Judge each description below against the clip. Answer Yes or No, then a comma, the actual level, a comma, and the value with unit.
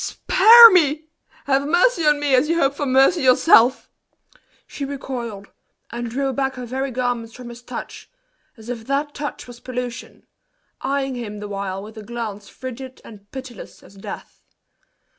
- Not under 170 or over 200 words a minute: No, average, 160 wpm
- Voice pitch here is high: Yes, very high, 255 Hz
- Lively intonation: No, average, 3.2 semitones